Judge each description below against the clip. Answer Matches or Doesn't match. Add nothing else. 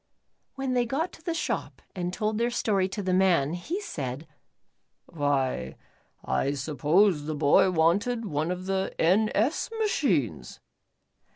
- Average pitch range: Doesn't match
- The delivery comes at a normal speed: Matches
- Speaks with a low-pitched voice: Doesn't match